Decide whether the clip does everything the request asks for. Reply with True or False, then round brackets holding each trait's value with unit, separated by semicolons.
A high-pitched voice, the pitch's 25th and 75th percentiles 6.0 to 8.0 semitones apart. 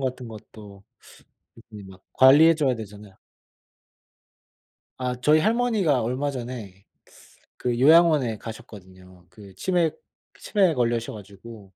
False (120 Hz; 6.3 semitones)